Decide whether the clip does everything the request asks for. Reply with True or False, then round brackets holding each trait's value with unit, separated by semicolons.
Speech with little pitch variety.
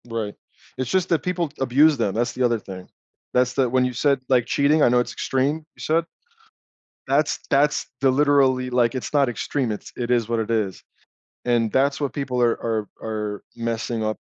False (3.3 semitones)